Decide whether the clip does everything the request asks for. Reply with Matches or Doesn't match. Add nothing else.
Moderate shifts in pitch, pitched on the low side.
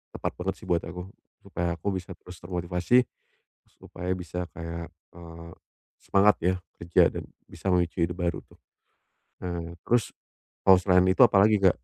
Doesn't match